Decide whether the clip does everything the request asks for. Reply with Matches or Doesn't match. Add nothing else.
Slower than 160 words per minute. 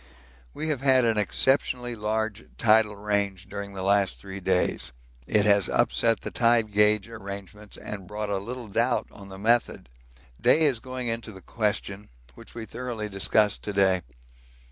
Doesn't match